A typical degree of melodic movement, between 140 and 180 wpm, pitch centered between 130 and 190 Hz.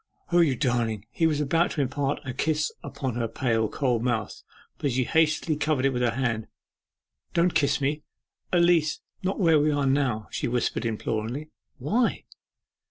Yes: average, 4.2 semitones; average, 165 wpm; medium, 140 Hz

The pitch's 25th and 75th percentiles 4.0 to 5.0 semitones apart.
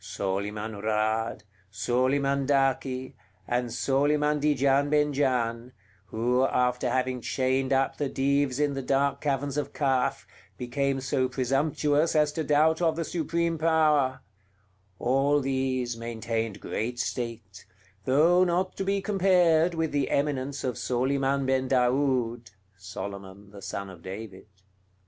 No: average, 3.2 semitones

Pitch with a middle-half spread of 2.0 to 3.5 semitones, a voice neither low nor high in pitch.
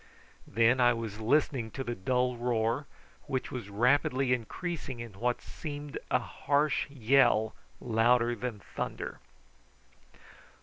No: average, 2.9 semitones; low, 125 Hz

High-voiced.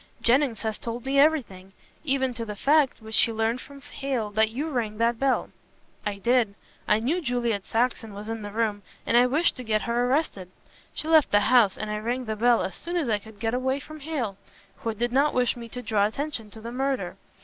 Yes: high, 235 Hz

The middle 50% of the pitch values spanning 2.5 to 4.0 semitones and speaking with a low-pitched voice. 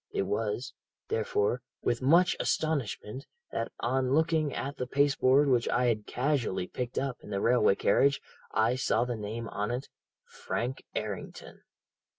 Yes: average, 3.6 semitones; low, 125 Hz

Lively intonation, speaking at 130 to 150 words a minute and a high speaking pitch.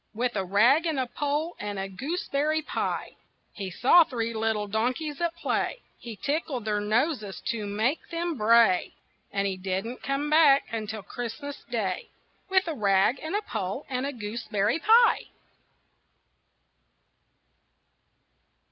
Yes: wide, 6.2 semitones; average, 140 wpm; high, 240 Hz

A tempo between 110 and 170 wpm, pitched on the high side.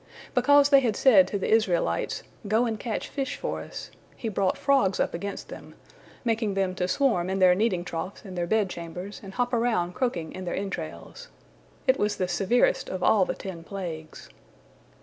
No: average, 190 wpm; high, 195 Hz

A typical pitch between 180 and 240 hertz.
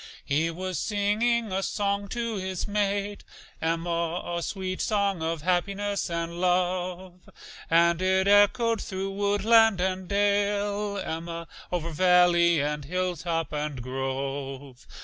Yes: medium, 185 Hz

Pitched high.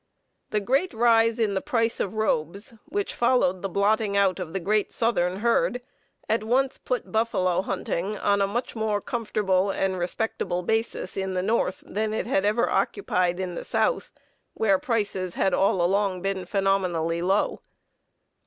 Yes: high, 200 Hz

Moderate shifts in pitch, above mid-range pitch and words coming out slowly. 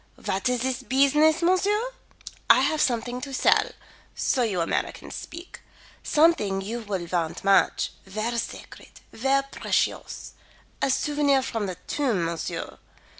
No: wide, 6.6 semitones; very high, 250 Hz; slow, 130 wpm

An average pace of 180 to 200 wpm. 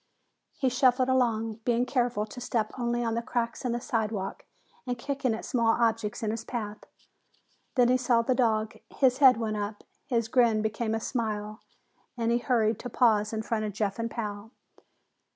Yes: average, 185 wpm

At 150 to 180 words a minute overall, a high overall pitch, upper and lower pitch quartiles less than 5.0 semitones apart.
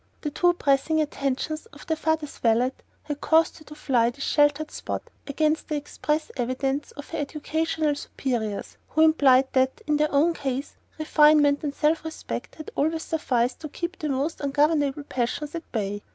Yes: average, 170 wpm; very high, 295 Hz; narrow, 2.6 semitones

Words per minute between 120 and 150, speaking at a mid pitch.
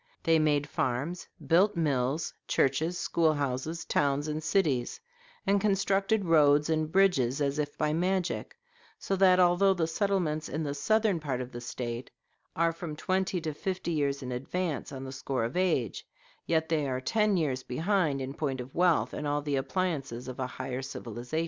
No: average, 175 wpm; medium, 155 Hz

